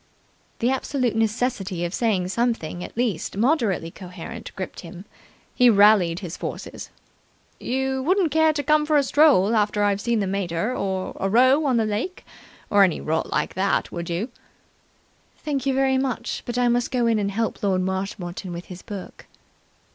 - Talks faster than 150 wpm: Yes, average, 175 wpm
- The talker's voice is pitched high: Yes, high, 215 Hz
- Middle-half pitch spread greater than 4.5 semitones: Yes, wide, 5.5 semitones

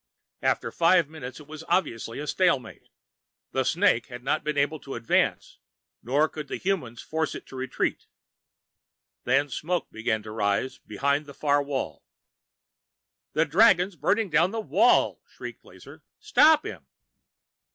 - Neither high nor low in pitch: Yes, medium, 145 Hz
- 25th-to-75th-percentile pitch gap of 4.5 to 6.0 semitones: Yes, average, 5.0 semitones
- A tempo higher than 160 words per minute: No, average, 145 wpm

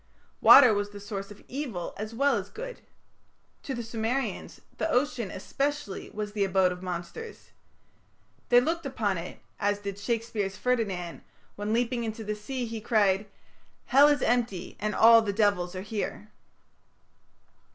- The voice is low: No, high, 215 Hz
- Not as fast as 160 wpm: Yes, average, 150 wpm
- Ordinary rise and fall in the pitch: Yes, average, 3.6 semitones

